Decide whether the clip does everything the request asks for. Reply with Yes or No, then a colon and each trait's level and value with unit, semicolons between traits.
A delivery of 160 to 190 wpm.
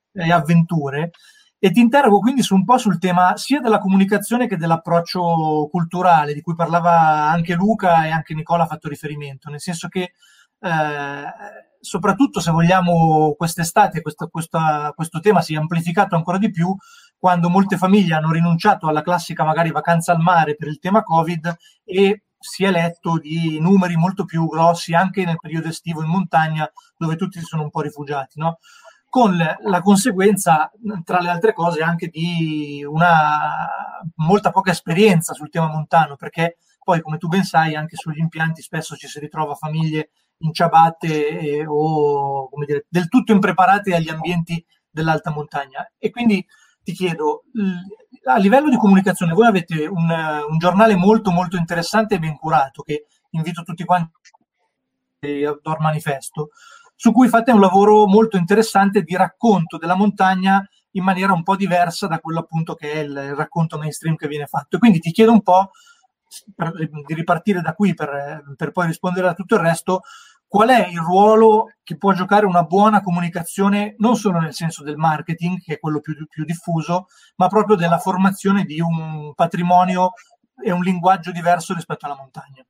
Yes: fast, 170 wpm